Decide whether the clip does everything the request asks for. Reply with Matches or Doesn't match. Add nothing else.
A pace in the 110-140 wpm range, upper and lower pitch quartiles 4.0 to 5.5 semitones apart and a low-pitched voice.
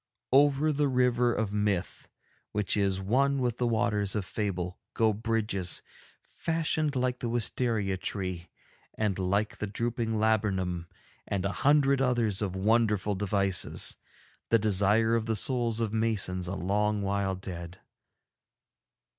Doesn't match